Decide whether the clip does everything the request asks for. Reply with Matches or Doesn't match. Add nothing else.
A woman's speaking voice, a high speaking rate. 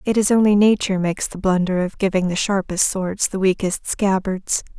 Doesn't match